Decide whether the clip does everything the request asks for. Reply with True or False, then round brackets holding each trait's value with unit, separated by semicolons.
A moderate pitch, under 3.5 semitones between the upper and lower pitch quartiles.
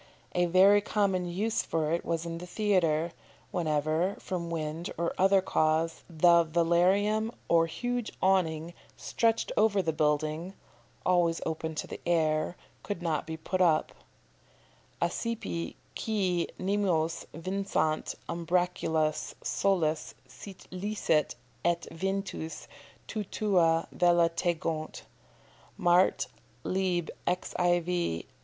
True (175 Hz; 2.8 semitones)